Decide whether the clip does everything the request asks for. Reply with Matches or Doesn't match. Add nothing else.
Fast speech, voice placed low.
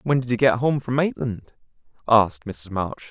Doesn't match